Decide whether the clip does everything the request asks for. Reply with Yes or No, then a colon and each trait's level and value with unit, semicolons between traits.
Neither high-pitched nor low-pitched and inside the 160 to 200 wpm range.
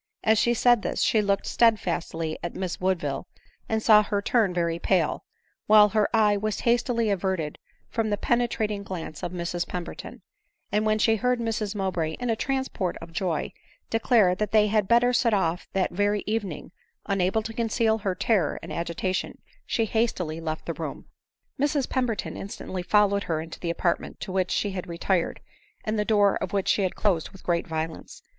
No: high, 200 Hz; average, 185 wpm